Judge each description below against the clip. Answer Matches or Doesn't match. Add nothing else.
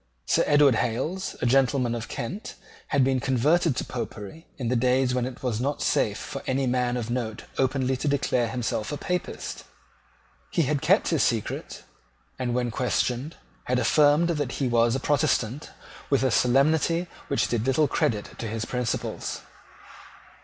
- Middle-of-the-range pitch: Doesn't match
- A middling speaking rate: Matches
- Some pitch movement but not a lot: Matches